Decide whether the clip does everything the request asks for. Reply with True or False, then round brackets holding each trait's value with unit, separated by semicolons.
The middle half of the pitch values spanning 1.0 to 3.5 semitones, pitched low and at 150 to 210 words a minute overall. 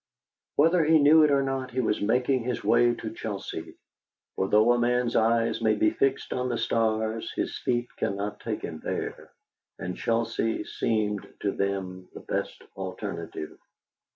True (3.2 semitones; 115 Hz; 160 wpm)